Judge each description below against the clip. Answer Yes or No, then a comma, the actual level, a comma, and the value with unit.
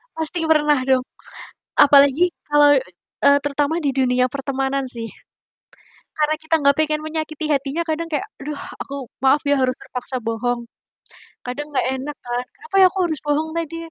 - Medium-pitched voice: No, very high, 290 Hz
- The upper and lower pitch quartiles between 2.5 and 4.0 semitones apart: Yes, average, 2.9 semitones